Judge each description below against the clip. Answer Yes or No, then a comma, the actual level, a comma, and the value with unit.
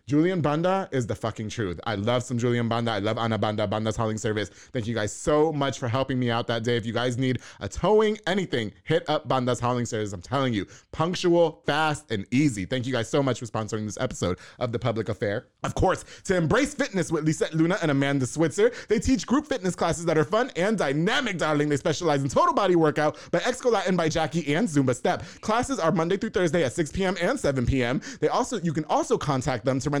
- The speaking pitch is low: No, medium, 145 Hz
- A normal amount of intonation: No, wide, 6.2 semitones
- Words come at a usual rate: No, fast, 235 wpm